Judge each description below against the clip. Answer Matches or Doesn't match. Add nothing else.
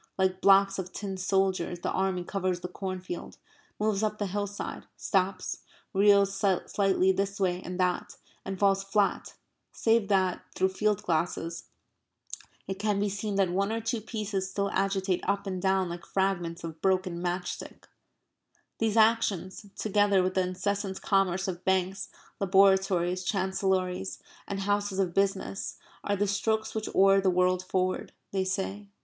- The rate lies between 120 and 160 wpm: Matches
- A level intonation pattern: Matches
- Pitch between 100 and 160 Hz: Doesn't match